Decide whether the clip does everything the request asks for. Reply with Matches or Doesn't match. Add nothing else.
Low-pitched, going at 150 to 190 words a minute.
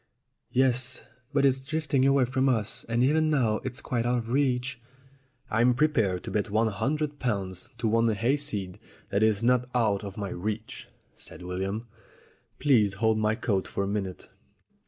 Matches